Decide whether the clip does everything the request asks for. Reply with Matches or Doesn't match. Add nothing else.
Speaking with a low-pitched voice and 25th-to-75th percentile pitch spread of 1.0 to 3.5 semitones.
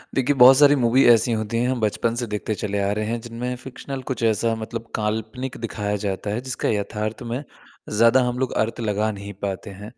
Matches